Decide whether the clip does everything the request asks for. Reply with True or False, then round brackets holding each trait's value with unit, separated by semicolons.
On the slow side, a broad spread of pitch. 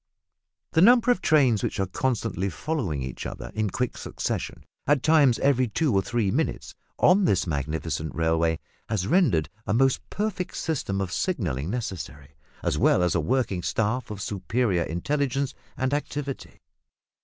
False (155 wpm; 8.0 semitones)